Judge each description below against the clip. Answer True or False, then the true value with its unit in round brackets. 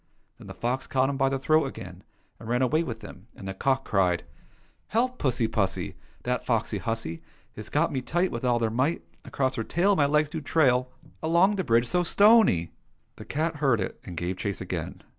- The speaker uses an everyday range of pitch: False (5.7 semitones)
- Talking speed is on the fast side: True (220 wpm)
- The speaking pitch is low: True (130 Hz)